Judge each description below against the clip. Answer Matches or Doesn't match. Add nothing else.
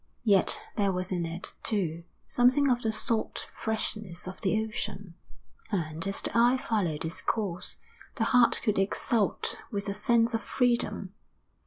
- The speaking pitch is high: Matches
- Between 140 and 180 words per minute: Matches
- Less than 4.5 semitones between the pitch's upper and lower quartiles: Matches